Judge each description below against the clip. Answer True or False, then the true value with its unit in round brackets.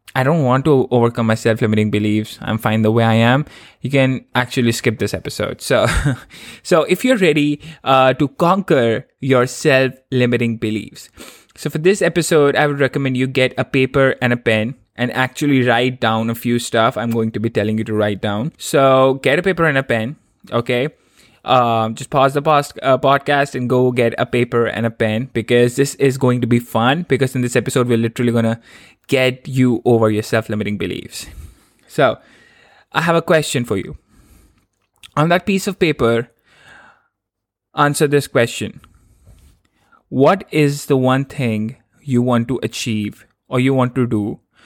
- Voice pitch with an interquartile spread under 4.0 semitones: True (3.4 semitones)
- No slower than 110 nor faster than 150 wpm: False (180 wpm)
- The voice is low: True (125 Hz)